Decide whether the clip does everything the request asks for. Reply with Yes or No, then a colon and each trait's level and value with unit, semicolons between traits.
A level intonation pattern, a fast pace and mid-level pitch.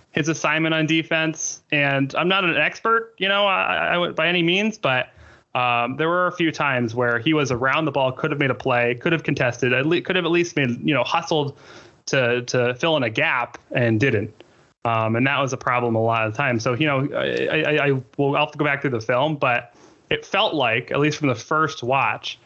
No: average, 4.3 semitones; fast, 245 wpm; medium, 145 Hz